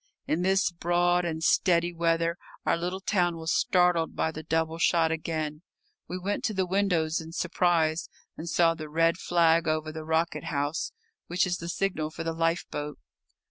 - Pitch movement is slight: Yes, narrow, 1.6 semitones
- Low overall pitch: No, medium, 165 Hz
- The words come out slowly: No, average, 175 wpm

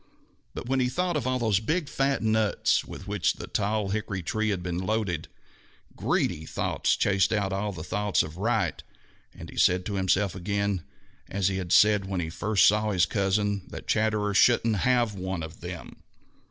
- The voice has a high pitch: No, low, 100 Hz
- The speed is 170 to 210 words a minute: Yes, average, 180 wpm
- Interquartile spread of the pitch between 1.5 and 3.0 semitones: Yes, narrow, 2.6 semitones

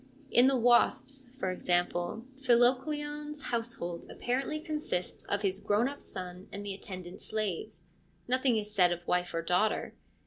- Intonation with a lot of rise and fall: Yes, wide, 6.3 semitones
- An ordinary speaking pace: Yes, average, 145 wpm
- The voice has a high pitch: Yes, high, 215 Hz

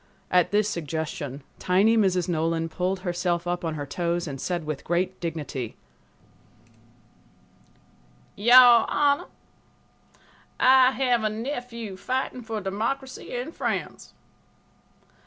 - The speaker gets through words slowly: Yes, slow, 110 wpm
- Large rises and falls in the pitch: Yes, wide, 6.1 semitones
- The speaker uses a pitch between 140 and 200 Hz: Yes, high, 190 Hz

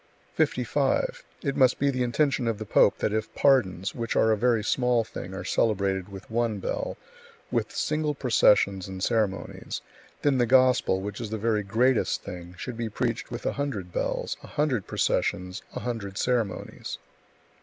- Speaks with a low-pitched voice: Yes, low, 115 Hz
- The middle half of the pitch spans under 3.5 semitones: No, average, 4.2 semitones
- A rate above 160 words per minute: Yes, average, 170 wpm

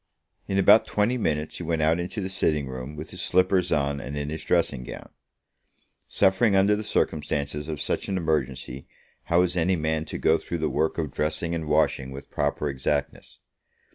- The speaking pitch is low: Yes, very low, 80 Hz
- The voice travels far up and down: No, average, 3.8 semitones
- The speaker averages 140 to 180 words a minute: No, average, 190 wpm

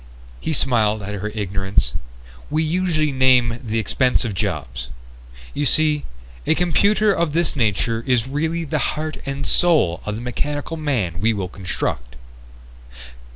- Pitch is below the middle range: Yes, low, 125 Hz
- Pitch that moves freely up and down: Yes, wide, 6.9 semitones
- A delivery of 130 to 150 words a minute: Yes, average, 140 wpm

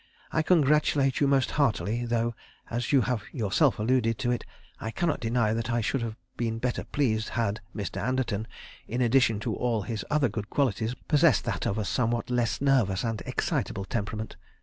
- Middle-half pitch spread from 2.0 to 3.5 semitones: Yes, average, 3.0 semitones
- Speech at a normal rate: Yes, average, 180 wpm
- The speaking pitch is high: No, low, 120 Hz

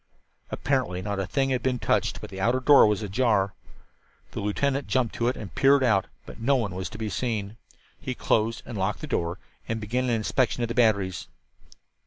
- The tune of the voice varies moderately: Yes, average, 4.1 semitones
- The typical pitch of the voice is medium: No, low, 115 Hz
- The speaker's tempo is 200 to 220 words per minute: Yes, fast, 205 wpm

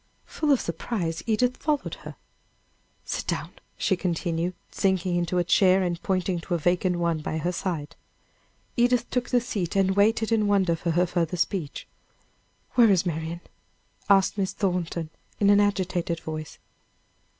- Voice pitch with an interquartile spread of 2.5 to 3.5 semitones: Yes, average, 3.2 semitones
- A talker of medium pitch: Yes, medium, 180 Hz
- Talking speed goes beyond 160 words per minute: No, average, 155 wpm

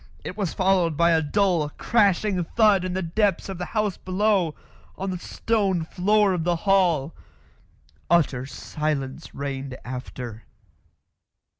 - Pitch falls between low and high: Yes, medium, 180 Hz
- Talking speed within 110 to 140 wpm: Yes, slow, 135 wpm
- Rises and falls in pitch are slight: No, average, 4.3 semitones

